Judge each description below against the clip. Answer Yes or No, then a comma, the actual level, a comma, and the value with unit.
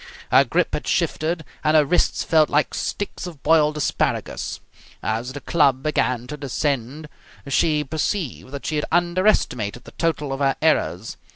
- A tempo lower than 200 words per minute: Yes, average, 160 wpm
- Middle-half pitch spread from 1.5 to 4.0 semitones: Yes, average, 3.2 semitones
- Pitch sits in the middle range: Yes, medium, 150 Hz